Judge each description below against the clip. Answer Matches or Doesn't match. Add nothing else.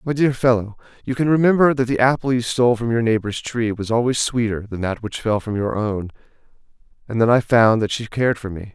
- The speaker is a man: Matches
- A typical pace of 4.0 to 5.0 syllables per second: Doesn't match